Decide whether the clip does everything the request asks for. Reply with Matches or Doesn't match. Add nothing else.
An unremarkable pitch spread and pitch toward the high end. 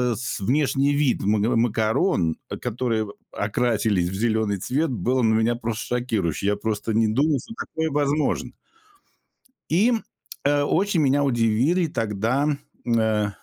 Doesn't match